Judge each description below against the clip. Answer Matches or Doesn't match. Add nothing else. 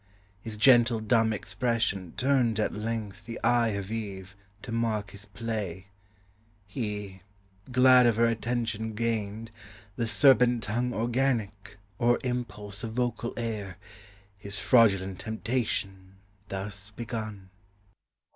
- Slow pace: Matches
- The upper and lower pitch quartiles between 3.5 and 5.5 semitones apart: Doesn't match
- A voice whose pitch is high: Doesn't match